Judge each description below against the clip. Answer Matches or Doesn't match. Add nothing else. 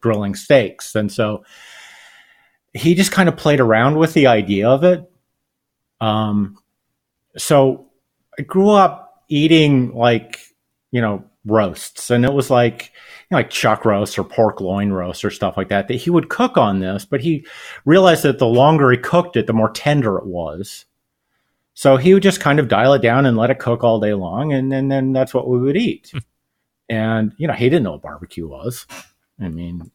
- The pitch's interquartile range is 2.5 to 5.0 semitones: Doesn't match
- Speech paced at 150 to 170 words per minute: Doesn't match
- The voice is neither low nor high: Doesn't match